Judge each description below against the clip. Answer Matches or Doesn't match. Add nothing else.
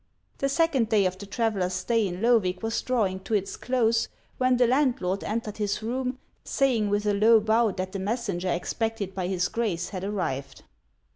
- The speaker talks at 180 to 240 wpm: Matches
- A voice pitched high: Matches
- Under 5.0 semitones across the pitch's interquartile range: Matches